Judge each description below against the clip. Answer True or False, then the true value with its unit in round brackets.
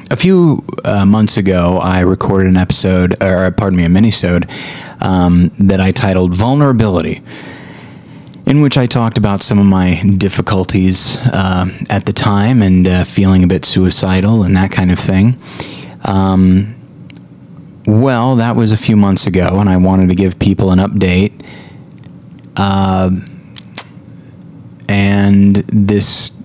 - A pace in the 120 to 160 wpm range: True (140 wpm)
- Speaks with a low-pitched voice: True (95 Hz)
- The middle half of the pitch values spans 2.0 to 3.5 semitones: True (2.5 semitones)